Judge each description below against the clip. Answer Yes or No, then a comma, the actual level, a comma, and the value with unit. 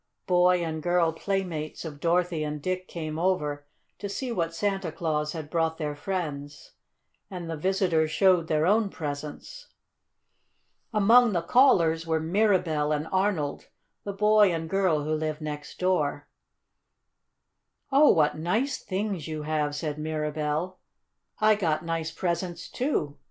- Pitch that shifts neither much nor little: Yes, average, 3.7 semitones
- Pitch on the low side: No, medium, 165 Hz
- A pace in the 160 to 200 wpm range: No, average, 140 wpm